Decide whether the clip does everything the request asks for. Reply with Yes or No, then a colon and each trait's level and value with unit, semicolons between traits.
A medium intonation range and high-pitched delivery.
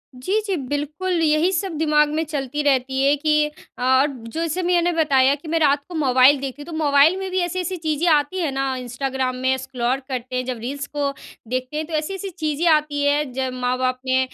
Yes: average, 3.5 semitones; very high, 290 Hz